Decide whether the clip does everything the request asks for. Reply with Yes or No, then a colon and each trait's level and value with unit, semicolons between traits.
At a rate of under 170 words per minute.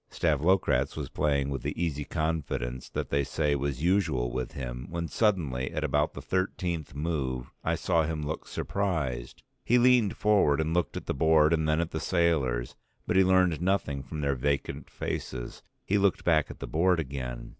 No: average, 185 wpm